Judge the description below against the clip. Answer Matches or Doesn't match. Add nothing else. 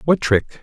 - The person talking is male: Matches